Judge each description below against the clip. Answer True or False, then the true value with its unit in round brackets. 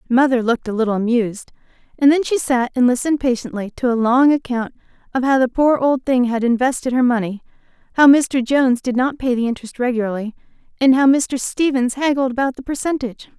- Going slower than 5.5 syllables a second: False (6.0 syllables/s)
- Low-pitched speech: False (255 Hz)